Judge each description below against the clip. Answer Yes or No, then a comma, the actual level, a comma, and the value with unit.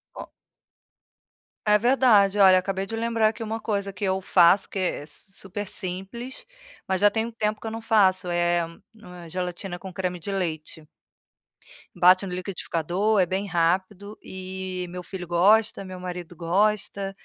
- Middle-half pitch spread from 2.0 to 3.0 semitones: Yes, average, 2.7 semitones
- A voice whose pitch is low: No, high, 190 Hz